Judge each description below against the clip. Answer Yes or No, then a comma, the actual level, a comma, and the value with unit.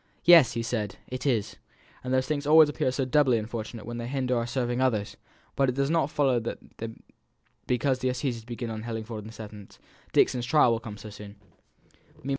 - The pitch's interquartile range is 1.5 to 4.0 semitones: Yes, average, 2.8 semitones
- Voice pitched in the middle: No, low, 120 Hz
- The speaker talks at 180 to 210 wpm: Yes, average, 200 wpm